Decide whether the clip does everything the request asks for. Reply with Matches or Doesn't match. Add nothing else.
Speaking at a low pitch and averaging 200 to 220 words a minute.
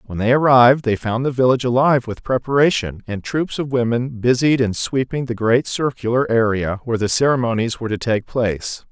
Doesn't match